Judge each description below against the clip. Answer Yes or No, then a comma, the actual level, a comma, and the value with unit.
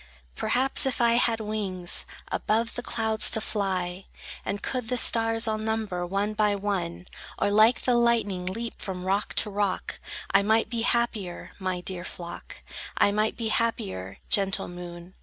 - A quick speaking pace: No, average, 160 wpm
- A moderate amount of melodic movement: Yes, average, 3.5 semitones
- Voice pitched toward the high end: Yes, high, 210 Hz